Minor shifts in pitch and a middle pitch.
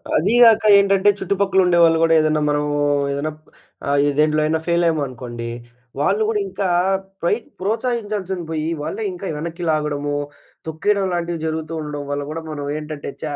No: average, 4.3 semitones; medium, 165 Hz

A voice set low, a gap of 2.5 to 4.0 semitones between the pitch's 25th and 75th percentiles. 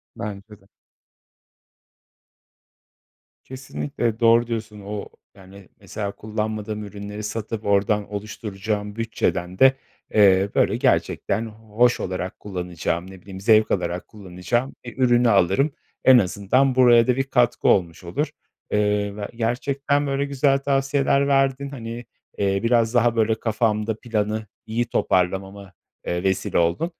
Yes: low, 110 Hz; average, 3.5 semitones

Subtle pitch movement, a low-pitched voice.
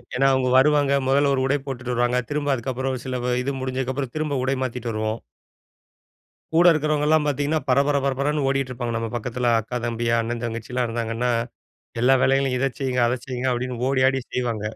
Yes: narrow, 2.3 semitones; low, 130 Hz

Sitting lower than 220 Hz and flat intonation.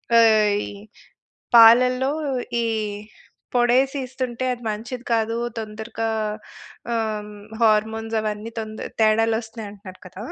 No: high, 225 Hz; narrow, 1.8 semitones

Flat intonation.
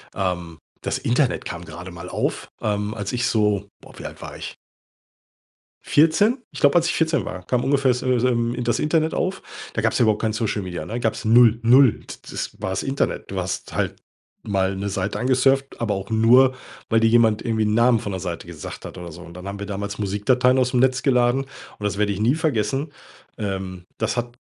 No: average, 4.4 semitones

